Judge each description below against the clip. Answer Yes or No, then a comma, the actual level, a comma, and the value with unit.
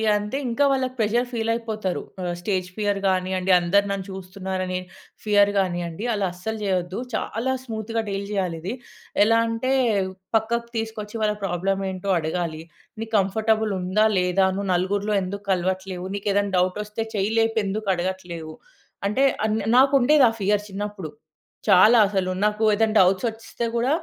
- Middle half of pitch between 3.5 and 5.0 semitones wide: No, average, 3.0 semitones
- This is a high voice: Yes, high, 200 Hz